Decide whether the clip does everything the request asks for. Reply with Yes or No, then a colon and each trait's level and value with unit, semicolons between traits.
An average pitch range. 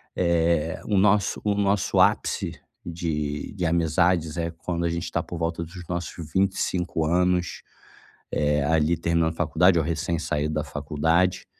No: narrow, 2.0 semitones